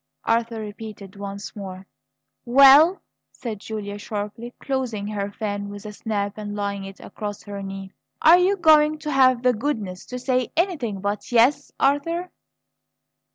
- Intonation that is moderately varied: Yes, average, 4.9 semitones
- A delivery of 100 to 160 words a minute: Yes, average, 150 wpm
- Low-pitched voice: No, high, 220 Hz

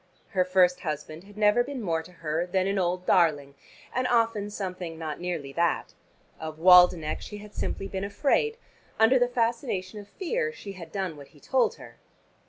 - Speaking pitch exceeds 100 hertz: Yes, medium, 185 Hz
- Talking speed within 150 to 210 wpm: Yes, average, 185 wpm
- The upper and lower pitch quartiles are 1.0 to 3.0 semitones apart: No, average, 4.4 semitones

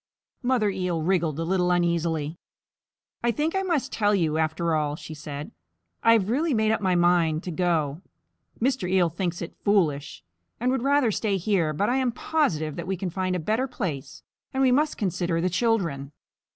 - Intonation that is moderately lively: No, wide, 5.9 semitones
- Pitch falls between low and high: Yes, medium, 180 Hz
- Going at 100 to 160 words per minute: No, average, 190 wpm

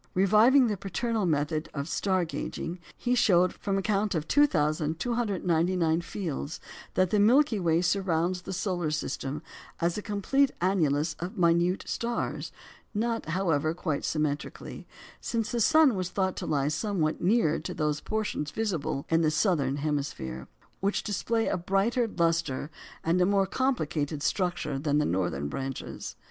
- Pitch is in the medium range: Yes, medium, 175 Hz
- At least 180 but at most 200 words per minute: No, average, 150 wpm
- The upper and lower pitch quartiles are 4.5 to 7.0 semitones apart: Yes, average, 5.0 semitones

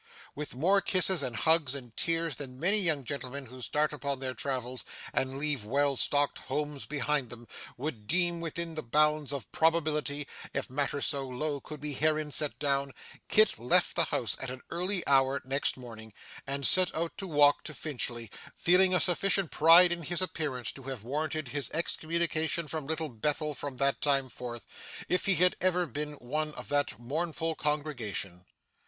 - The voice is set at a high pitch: No, medium, 145 Hz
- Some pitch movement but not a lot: Yes, average, 3.5 semitones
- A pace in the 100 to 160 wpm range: No, average, 175 wpm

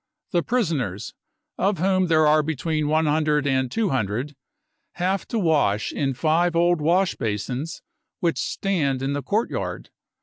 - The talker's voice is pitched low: No, medium, 155 Hz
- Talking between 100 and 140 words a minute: Yes, slow, 135 wpm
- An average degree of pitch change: Yes, average, 4.4 semitones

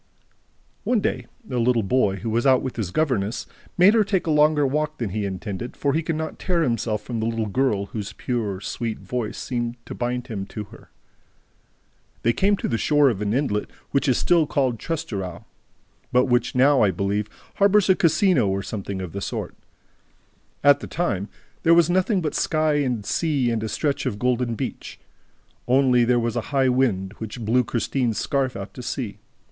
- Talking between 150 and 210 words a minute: Yes, average, 195 wpm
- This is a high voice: No, low, 125 Hz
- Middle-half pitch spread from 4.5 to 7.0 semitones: Yes, wide, 5.4 semitones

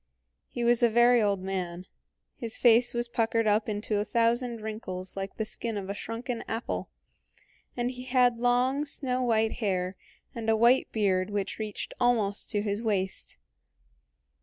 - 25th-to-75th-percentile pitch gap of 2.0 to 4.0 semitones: Yes, average, 2.8 semitones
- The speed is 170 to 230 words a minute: No, average, 160 wpm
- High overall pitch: Yes, high, 225 Hz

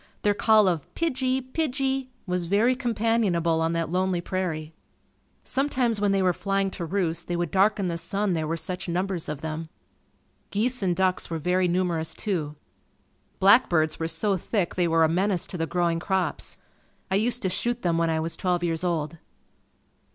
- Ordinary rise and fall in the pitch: Yes, average, 3.8 semitones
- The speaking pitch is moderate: Yes, medium, 180 Hz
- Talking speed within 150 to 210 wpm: Yes, average, 180 wpm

